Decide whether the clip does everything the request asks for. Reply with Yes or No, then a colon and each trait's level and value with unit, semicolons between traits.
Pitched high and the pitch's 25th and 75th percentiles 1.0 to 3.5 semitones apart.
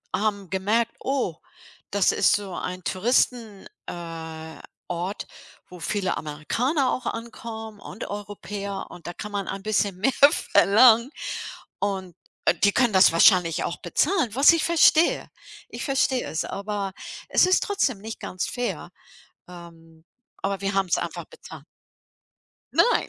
No: high, 200 Hz; average, 4.4 semitones